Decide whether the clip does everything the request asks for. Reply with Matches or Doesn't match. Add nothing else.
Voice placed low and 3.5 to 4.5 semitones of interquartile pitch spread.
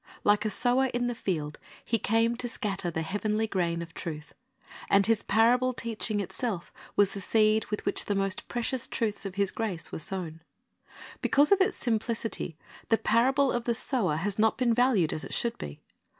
Doesn't match